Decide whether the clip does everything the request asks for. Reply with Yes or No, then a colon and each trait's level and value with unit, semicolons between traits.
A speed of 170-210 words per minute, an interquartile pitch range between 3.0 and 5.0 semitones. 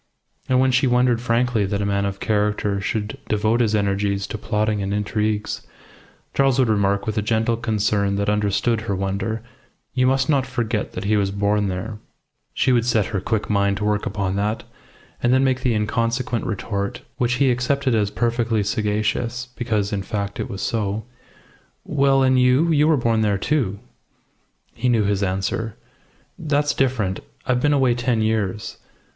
Yes: average, 175 wpm; average, 3.4 semitones